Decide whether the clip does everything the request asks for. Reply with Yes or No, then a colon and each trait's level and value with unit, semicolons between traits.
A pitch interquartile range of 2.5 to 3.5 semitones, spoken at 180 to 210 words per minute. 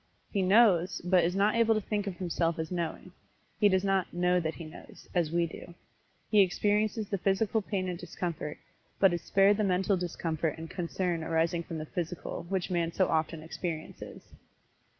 Yes: average, 2.8 semitones; average, 185 wpm